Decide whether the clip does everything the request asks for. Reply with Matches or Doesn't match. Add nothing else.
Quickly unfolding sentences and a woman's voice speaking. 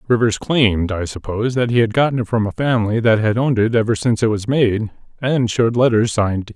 Doesn't match